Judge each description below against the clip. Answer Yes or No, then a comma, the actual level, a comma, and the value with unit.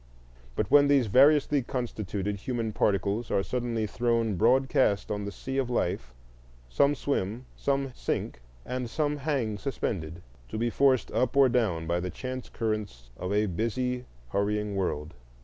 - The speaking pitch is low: Yes, low, 115 Hz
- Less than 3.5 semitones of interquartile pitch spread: No, average, 4.4 semitones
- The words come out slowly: No, average, 150 wpm